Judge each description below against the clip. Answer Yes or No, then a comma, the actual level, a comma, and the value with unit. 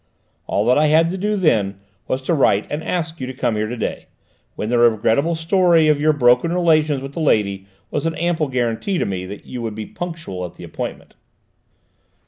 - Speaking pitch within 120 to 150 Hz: Yes, medium, 140 Hz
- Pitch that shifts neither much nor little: No, wide, 6.6 semitones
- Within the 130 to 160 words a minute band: No, fast, 205 wpm